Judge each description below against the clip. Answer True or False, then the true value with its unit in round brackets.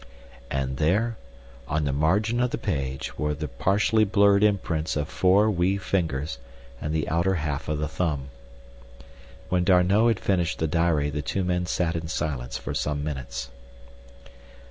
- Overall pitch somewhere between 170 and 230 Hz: False (80 Hz)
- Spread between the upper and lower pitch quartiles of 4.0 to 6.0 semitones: True (4.6 semitones)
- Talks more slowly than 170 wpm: True (160 wpm)